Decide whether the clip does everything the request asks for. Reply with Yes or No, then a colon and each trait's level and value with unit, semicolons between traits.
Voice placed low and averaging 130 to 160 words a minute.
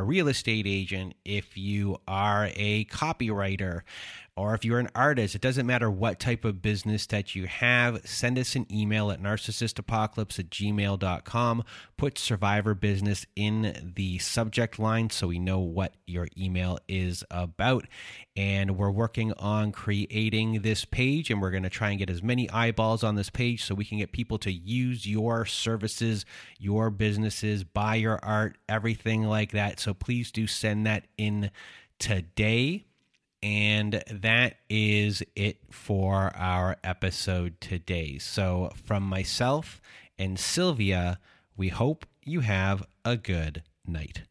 Yes: low, 105 Hz; average, 150 wpm